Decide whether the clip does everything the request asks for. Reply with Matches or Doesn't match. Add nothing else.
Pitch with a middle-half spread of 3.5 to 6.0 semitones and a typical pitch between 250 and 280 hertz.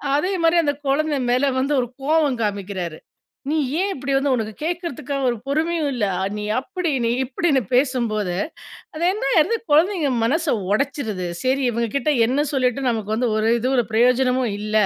Matches